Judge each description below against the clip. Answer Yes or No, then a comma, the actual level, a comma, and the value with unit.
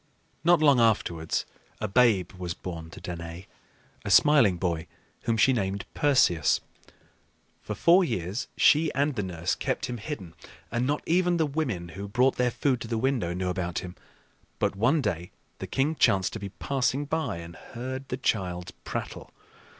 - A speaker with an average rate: Yes, average, 170 wpm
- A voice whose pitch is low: Yes, low, 110 Hz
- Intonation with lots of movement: Yes, wide, 7.3 semitones